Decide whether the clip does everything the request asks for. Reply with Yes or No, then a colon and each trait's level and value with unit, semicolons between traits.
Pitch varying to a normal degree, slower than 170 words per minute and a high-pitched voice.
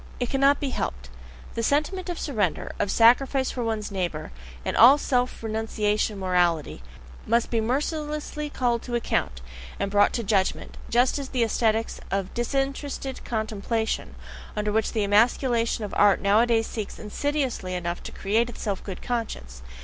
Yes: average, 4.1 semitones; average, 155 wpm; high, 225 Hz